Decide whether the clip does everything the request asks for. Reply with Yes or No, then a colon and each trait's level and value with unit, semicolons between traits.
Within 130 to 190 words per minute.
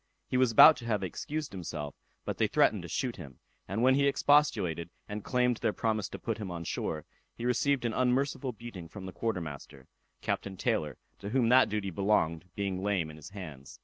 No: fast, 205 wpm